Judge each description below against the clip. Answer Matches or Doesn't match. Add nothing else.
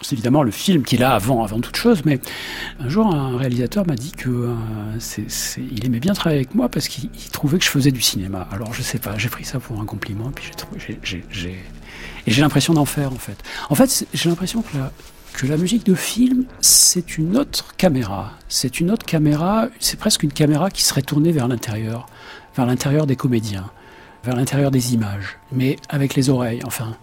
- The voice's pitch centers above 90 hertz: Matches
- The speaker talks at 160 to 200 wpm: Doesn't match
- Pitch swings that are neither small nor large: Doesn't match